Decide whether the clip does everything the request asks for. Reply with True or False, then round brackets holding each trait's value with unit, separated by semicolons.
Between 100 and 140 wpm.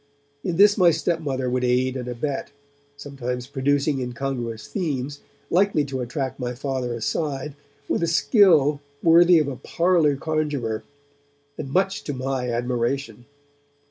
True (135 wpm)